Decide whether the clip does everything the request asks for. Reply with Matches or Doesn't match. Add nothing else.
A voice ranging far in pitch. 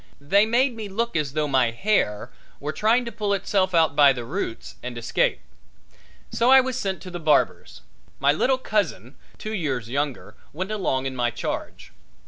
Matches